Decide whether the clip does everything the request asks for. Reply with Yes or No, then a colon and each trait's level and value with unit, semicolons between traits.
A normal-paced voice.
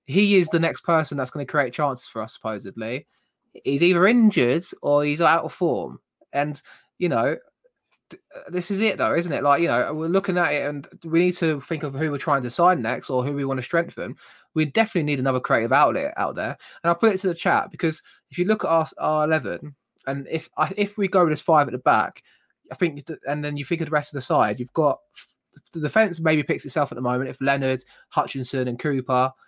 No: fast, 235 wpm